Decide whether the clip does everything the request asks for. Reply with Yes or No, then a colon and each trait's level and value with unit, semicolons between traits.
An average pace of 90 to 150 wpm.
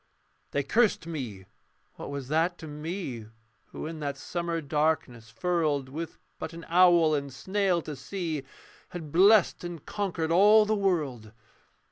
Yes: average, 145 wpm